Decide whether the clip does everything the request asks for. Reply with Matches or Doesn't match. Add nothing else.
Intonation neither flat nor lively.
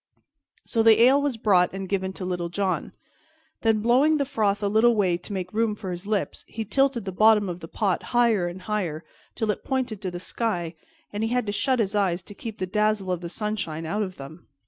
Matches